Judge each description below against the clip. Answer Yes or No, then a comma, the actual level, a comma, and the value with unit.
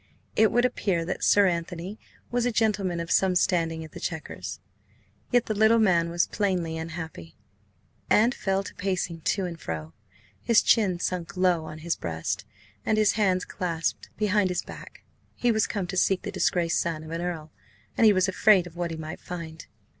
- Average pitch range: Yes, average, 3.8 semitones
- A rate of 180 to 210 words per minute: Yes, average, 190 wpm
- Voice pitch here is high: No, medium, 180 Hz